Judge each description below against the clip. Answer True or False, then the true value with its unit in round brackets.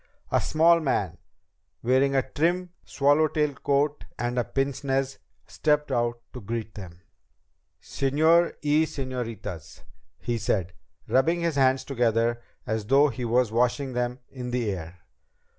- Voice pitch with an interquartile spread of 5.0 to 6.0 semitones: False (3.7 semitones)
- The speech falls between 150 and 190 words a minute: False (135 wpm)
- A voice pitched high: False (130 Hz)